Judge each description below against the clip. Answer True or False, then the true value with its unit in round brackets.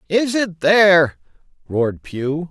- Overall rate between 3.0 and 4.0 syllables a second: True (3.8 syllables/s)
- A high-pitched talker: False (170 Hz)